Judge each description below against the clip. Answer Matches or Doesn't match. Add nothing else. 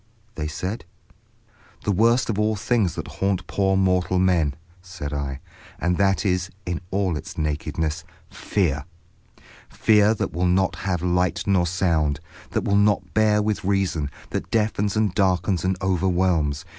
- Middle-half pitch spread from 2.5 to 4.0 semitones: Matches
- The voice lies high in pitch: Doesn't match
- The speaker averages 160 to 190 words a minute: Doesn't match